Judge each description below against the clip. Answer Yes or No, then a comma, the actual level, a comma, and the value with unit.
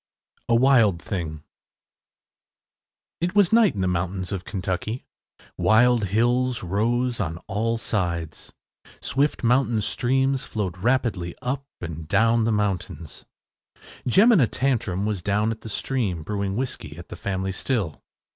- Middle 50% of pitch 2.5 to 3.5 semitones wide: No, average, 5.1 semitones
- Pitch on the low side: Yes, low, 110 Hz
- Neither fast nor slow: No, slow, 130 wpm